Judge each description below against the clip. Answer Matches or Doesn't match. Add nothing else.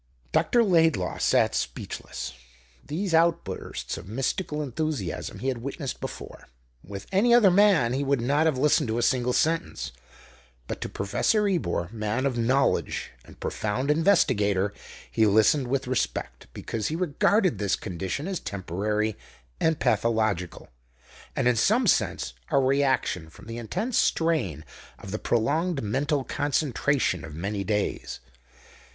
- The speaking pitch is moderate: Doesn't match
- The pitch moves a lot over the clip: Matches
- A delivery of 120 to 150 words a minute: Matches